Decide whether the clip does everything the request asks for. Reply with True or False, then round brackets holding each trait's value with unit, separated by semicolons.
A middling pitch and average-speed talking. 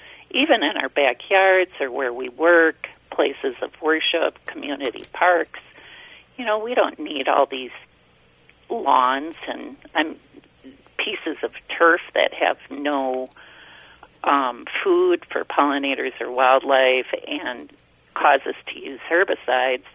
False (160 Hz; 125 wpm)